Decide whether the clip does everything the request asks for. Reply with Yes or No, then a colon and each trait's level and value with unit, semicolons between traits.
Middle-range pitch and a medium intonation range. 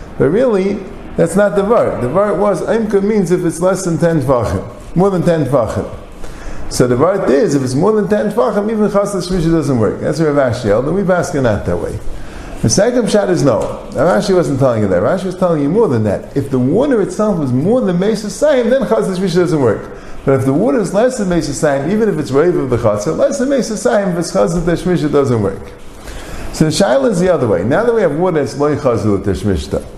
No: medium, 180 Hz; wide, 6.5 semitones